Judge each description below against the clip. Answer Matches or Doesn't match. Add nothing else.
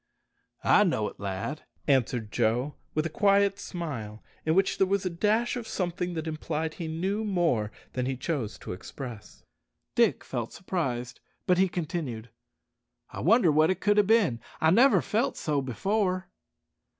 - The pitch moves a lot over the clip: Matches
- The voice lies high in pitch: Doesn't match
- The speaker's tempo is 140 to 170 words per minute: Matches